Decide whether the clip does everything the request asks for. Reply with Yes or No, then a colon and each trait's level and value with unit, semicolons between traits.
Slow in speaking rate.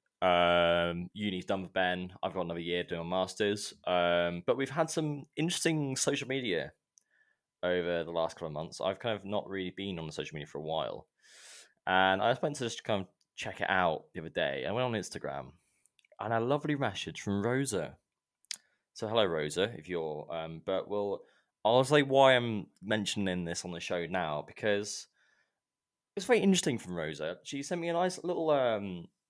No: average, 195 wpm